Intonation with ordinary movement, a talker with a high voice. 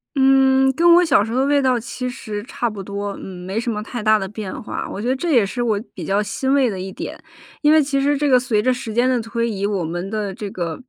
Yes: average, 4.7 semitones; high, 230 Hz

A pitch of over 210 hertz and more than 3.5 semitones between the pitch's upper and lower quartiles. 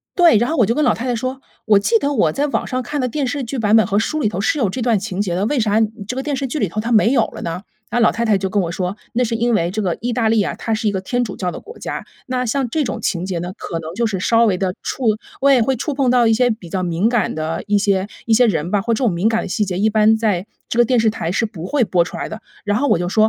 Yes: high, 220 Hz; average, 4.3 semitones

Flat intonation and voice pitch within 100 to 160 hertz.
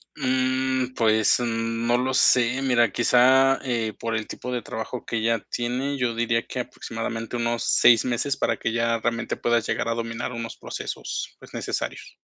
Yes: narrow, 1.8 semitones; low, 120 Hz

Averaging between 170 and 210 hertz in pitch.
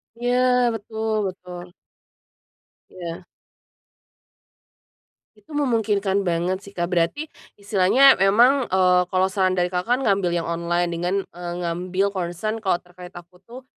Yes: medium, 185 Hz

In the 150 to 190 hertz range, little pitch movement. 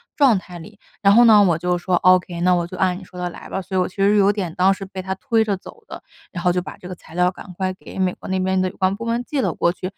Yes: medium, 185 Hz; narrow, 1.9 semitones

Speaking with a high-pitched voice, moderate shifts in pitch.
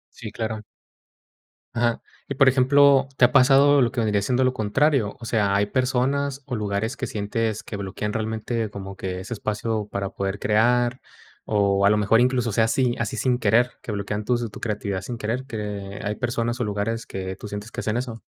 No: low, 110 Hz; average, 3.3 semitones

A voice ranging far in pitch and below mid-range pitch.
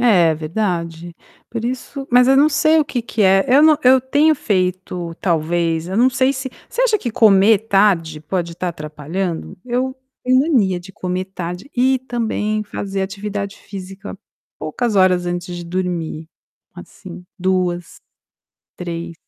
No: wide, 5.7 semitones; high, 195 Hz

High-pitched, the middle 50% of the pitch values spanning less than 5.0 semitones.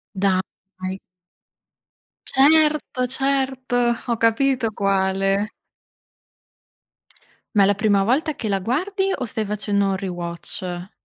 No: high, 210 Hz; average, 5.3 semitones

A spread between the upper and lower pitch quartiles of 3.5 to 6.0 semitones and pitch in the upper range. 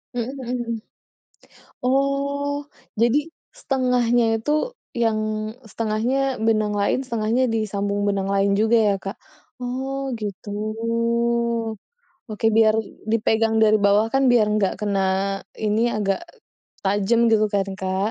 No: average, 3.0 semitones; high, 220 Hz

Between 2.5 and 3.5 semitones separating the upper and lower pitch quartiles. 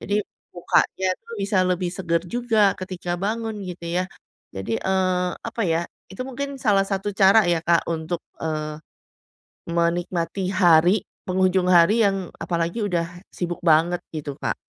Yes: average, 2.8 semitones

